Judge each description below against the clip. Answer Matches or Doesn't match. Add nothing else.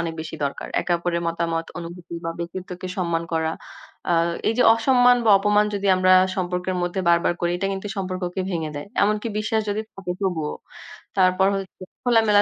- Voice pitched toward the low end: Doesn't match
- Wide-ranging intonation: Doesn't match